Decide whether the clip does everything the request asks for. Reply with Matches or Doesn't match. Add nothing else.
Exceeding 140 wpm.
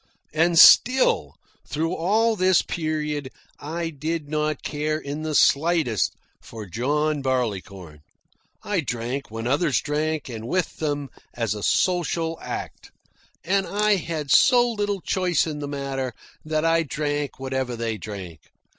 Doesn't match